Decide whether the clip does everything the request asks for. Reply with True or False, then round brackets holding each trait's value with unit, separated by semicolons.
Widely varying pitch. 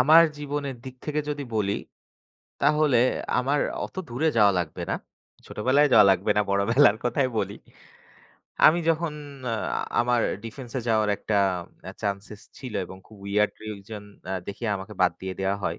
True (6.0 semitones)